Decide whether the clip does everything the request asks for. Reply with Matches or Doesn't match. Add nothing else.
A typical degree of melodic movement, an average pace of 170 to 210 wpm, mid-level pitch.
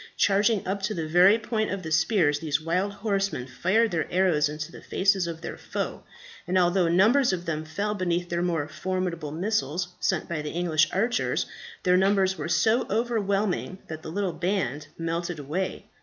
Matches